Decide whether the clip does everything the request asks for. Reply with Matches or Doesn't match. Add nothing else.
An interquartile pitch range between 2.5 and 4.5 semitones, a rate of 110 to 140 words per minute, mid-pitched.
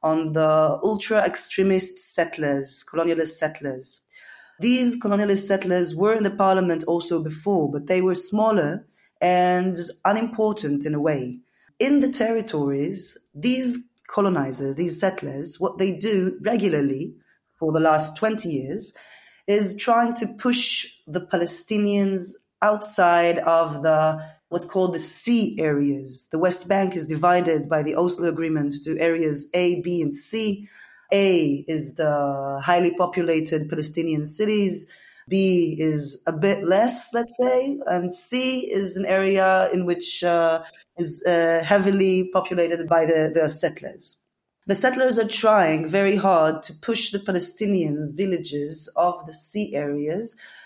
Matches